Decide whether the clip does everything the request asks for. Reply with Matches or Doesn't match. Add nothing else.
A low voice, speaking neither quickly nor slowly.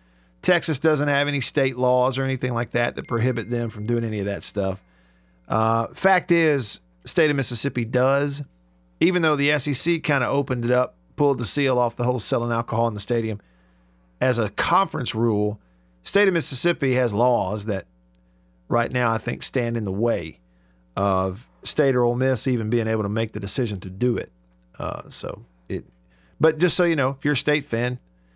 Matches